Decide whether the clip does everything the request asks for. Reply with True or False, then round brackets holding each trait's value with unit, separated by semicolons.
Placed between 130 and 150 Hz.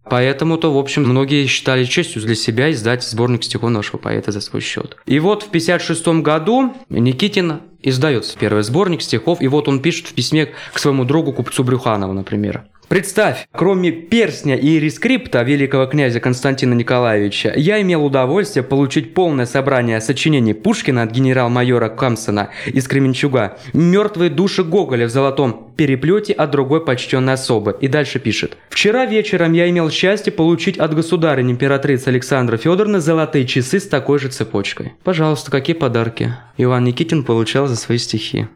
True (140 Hz)